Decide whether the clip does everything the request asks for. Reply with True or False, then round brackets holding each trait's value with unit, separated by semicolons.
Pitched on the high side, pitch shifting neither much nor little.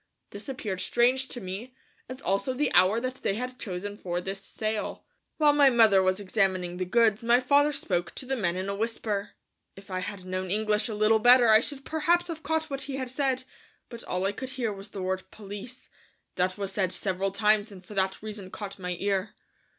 True (210 Hz; 4.9 semitones)